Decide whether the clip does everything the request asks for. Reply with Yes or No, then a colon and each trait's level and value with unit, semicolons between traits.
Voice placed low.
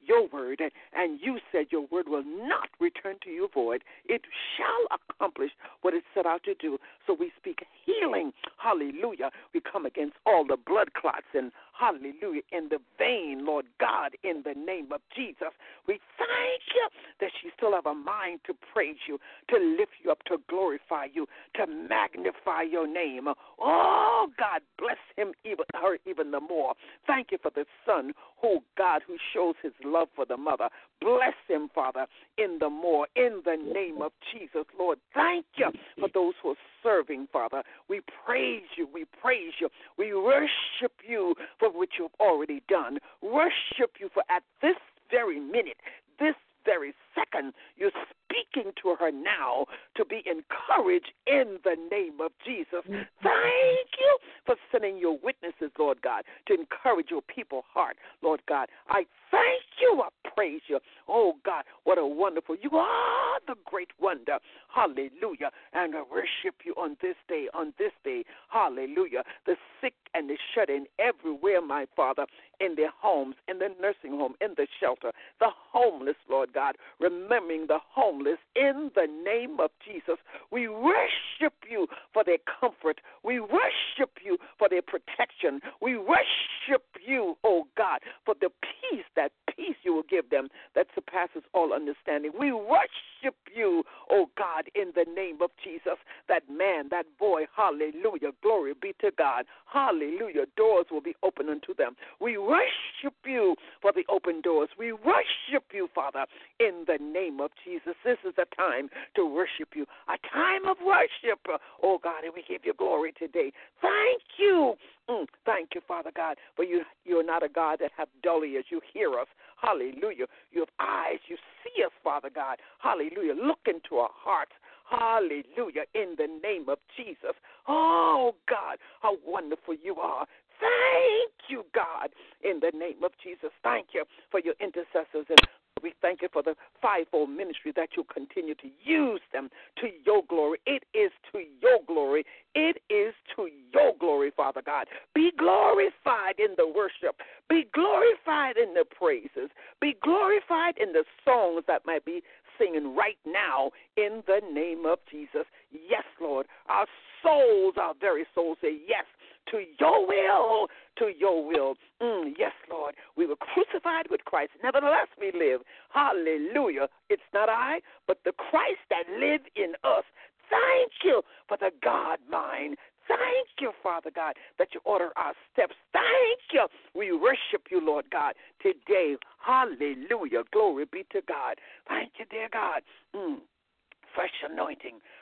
No: very high, 340 Hz